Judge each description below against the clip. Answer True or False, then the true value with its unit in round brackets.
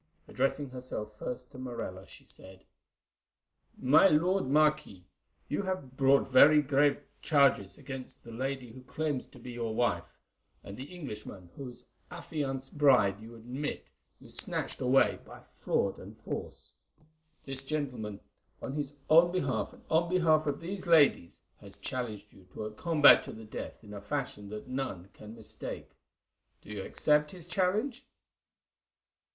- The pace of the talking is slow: False (150 wpm)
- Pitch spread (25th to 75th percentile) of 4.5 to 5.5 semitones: True (5.2 semitones)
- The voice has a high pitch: False (135 Hz)